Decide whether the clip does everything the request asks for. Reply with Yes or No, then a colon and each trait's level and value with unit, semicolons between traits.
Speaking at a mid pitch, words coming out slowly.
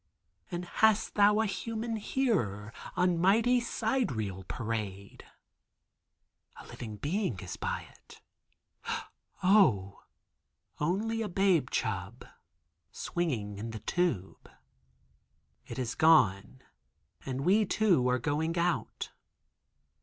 Yes: medium, 165 Hz; slow, 100 wpm